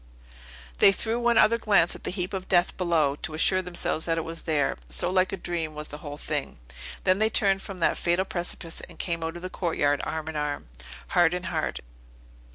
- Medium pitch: Yes, medium, 175 Hz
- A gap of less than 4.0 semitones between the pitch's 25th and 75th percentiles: Yes, average, 2.8 semitones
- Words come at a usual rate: No, fast, 215 wpm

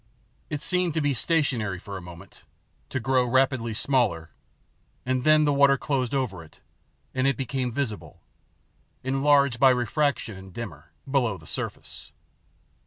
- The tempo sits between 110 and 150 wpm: Yes, average, 145 wpm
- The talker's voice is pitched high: No, low, 130 Hz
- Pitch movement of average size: Yes, average, 4.5 semitones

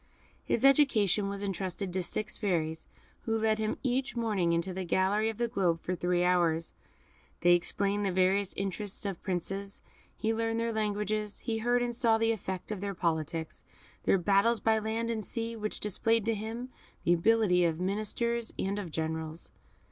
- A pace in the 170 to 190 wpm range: Yes, average, 175 wpm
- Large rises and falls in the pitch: No, average, 3.8 semitones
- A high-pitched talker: Yes, high, 205 Hz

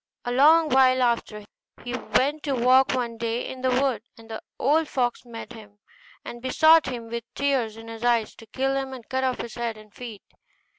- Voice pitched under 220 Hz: No, high, 245 Hz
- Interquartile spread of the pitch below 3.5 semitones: Yes, narrow, 2.5 semitones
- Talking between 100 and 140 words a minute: No, fast, 205 wpm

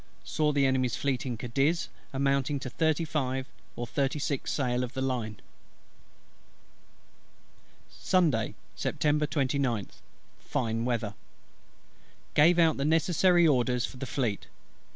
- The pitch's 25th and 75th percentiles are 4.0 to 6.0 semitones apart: No, average, 3.5 semitones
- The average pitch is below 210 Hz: Yes, low, 135 Hz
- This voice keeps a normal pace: No, slow, 120 wpm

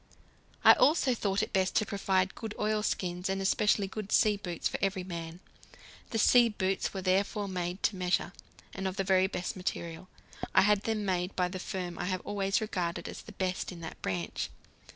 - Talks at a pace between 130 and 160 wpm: No, average, 195 wpm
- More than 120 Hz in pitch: Yes, high, 190 Hz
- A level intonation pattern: Yes, narrow, 2.3 semitones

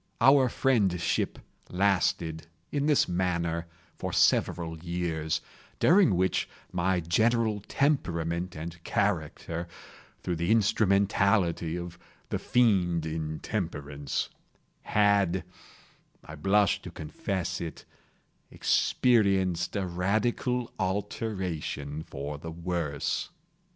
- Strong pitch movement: No, average, 3.7 semitones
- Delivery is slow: Yes, slow, 85 wpm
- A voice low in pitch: Yes, very low, 90 Hz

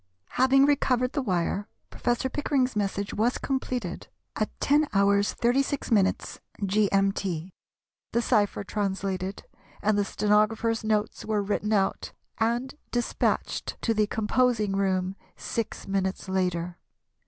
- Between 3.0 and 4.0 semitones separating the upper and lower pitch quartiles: Yes, average, 3.6 semitones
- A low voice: No, high, 210 Hz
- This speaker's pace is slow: Yes, slow, 110 wpm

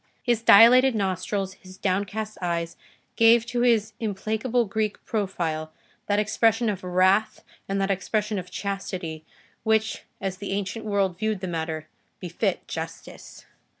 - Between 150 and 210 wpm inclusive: No, slow, 135 wpm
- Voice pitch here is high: Yes, high, 200 Hz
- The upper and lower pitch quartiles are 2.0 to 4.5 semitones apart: Yes, average, 2.8 semitones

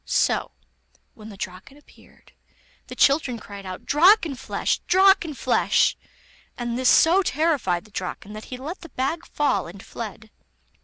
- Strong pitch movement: Yes, wide, 7.5 semitones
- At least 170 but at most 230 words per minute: No, average, 140 wpm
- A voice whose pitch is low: No, very high, 255 Hz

